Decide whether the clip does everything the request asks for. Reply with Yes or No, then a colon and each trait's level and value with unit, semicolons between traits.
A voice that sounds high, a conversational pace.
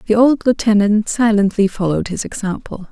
Yes: high, 210 Hz; average, 145 wpm